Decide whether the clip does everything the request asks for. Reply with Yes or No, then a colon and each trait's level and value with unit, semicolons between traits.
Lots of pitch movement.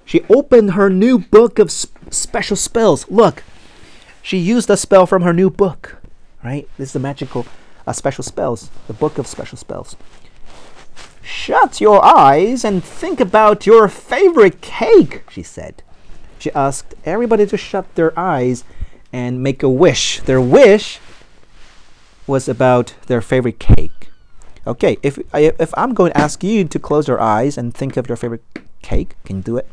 Yes: wide, 8.6 semitones